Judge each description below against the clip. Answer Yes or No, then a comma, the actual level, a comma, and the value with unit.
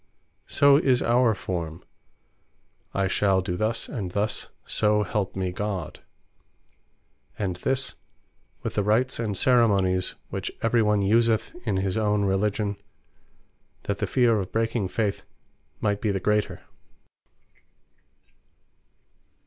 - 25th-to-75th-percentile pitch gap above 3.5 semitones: No, average, 2.9 semitones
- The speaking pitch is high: No, low, 105 Hz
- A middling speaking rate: No, slow, 120 wpm